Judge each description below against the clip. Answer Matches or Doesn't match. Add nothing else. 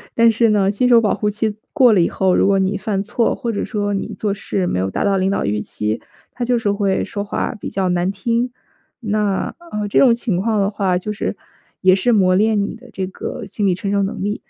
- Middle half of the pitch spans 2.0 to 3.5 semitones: Matches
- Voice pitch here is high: Matches